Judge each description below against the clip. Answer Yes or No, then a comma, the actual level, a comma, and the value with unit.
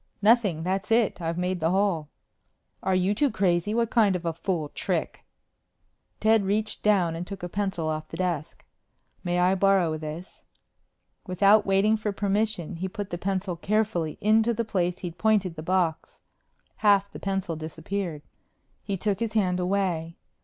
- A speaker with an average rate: Yes, average, 165 wpm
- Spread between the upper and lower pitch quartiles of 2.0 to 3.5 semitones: Yes, average, 3.2 semitones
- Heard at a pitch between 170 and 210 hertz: Yes, high, 190 Hz